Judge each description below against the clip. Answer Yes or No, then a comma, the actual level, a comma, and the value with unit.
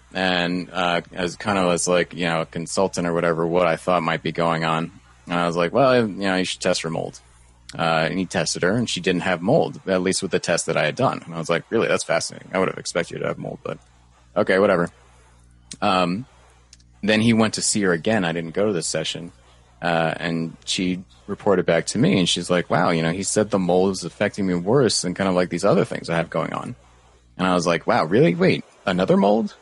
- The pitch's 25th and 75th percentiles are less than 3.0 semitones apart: Yes, narrow, 2.4 semitones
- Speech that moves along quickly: Yes, fast, 250 wpm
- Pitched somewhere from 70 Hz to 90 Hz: Yes, very low, 85 Hz